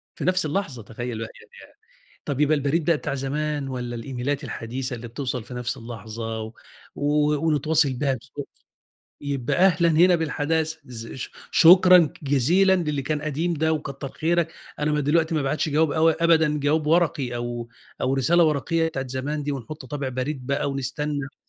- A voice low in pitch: No, medium, 145 Hz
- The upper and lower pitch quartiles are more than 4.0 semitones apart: No, average, 3.6 semitones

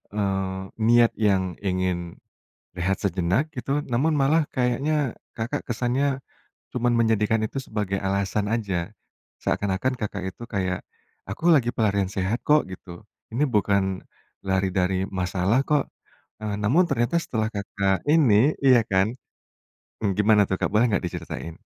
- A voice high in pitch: No, low, 105 Hz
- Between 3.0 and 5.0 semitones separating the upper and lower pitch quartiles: Yes, average, 3.9 semitones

